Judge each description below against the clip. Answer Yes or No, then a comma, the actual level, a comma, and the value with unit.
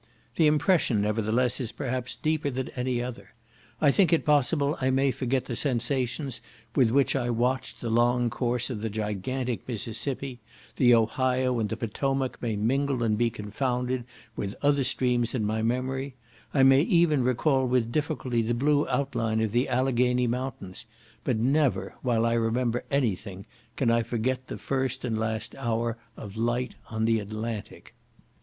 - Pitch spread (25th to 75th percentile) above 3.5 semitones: No, average, 2.7 semitones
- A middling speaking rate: Yes, average, 165 wpm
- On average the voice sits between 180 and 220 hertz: No, low, 125 Hz